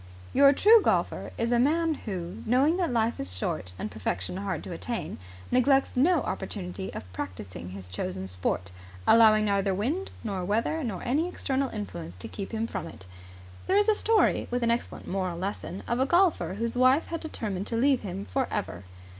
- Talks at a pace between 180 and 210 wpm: Yes, average, 190 wpm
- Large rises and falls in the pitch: Yes, wide, 7.1 semitones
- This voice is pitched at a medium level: No, high, 225 Hz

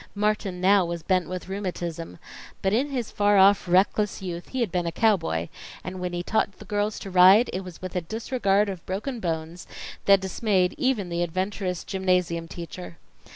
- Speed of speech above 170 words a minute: Yes, average, 185 wpm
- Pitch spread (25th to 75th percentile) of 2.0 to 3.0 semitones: Yes, average, 2.7 semitones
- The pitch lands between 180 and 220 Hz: Yes, medium, 185 Hz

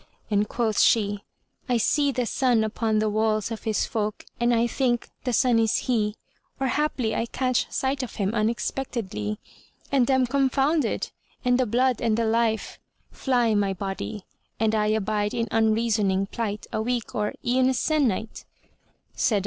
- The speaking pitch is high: Yes, high, 230 Hz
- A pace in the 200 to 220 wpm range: No, average, 160 wpm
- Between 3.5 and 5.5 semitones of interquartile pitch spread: No, average, 2.8 semitones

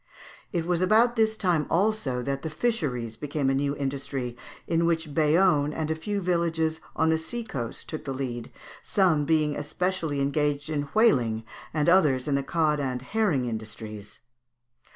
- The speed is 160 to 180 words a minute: Yes, average, 170 wpm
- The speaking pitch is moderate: Yes, medium, 150 Hz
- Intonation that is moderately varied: Yes, average, 4.0 semitones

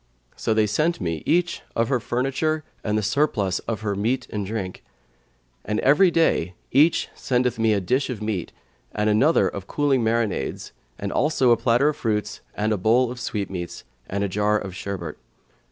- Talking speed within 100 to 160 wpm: No, average, 175 wpm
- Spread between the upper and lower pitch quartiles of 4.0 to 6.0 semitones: Yes, average, 4.3 semitones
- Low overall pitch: Yes, low, 110 Hz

